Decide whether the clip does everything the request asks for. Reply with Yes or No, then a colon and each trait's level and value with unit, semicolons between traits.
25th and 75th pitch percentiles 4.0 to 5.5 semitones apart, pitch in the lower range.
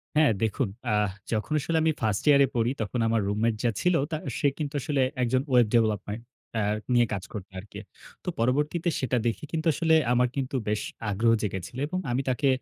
Yes: average, 5.0 semitones; low, 120 Hz